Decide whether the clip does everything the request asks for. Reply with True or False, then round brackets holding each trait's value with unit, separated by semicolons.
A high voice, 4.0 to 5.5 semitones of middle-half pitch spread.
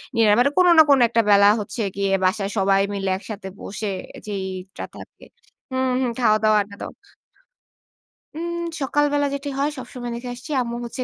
True (230 Hz; 4.6 semitones)